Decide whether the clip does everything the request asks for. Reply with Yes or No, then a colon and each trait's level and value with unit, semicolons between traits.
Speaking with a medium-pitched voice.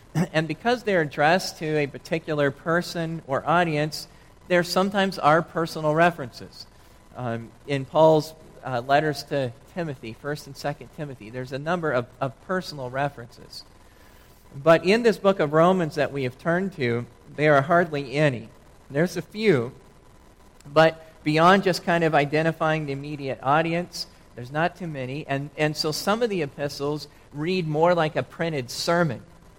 Yes: medium, 150 Hz